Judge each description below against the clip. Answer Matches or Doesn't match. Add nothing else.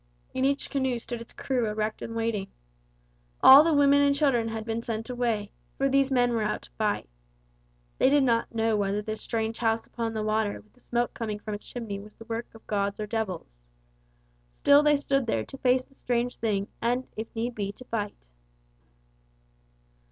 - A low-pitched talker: Doesn't match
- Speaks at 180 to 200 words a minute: Matches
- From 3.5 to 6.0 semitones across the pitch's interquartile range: Doesn't match